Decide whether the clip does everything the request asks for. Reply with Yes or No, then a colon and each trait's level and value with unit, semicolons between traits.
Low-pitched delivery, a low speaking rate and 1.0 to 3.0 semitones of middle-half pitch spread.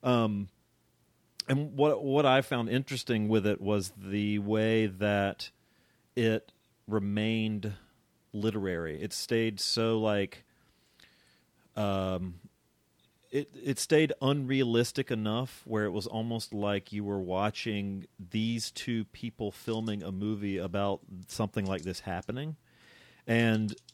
Yes: low, 110 Hz; slow, 115 wpm; narrow, 2.6 semitones